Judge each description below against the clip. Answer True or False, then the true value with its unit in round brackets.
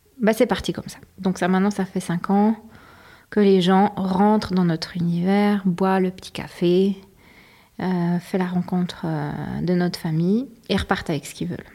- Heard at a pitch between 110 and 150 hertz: False (190 Hz)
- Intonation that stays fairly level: True (2.2 semitones)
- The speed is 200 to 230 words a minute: False (185 wpm)